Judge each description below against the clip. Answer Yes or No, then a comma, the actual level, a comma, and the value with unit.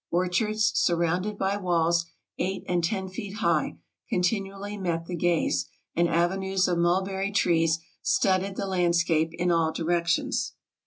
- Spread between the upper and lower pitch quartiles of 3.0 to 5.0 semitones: No, narrow, 2.4 semitones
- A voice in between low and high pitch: Yes, medium, 180 Hz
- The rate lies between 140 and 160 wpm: Yes, average, 145 wpm